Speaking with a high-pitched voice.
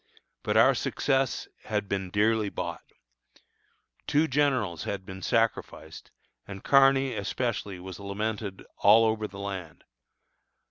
No: low, 105 Hz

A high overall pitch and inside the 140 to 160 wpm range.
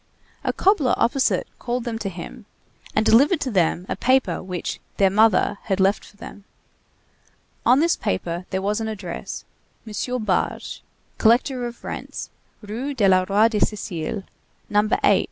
Yes: high, 215 Hz; average, 155 wpm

